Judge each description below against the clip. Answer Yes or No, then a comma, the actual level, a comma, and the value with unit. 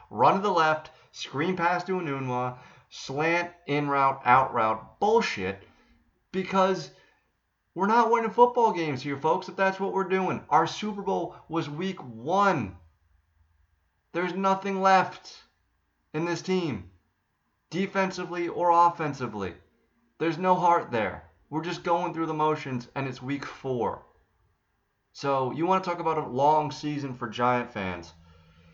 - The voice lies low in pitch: No, medium, 155 Hz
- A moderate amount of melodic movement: No, wide, 6.9 semitones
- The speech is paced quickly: No, average, 140 wpm